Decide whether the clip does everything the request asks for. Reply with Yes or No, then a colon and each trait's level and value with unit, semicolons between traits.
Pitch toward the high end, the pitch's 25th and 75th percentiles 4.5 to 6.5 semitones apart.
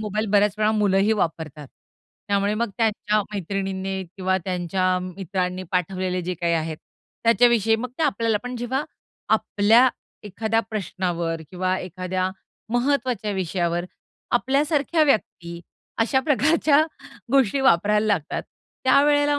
Yes: high, 205 Hz; average, 4.8 semitones